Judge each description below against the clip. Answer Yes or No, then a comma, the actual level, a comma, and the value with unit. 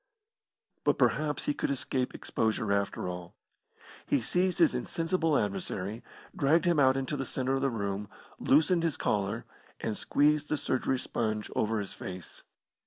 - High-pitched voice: No, low, 130 Hz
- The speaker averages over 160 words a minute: No, average, 155 wpm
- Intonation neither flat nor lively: No, wide, 6.1 semitones